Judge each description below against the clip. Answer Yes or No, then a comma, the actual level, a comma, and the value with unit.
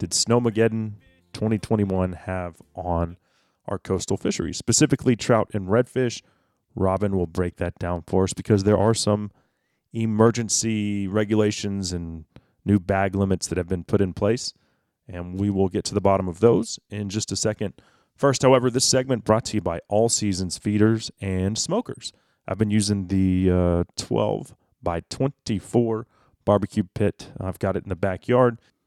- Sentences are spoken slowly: No, average, 160 wpm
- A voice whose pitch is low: Yes, low, 105 Hz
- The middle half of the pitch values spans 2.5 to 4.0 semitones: Yes, average, 3.2 semitones